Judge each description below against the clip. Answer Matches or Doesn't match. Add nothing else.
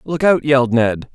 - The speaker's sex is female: Doesn't match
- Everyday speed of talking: Doesn't match